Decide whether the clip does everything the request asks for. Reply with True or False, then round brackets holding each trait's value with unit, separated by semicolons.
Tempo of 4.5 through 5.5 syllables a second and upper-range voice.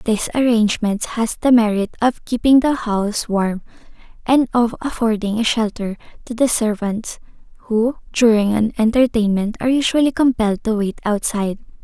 True (5.1 syllables/s; 225 Hz)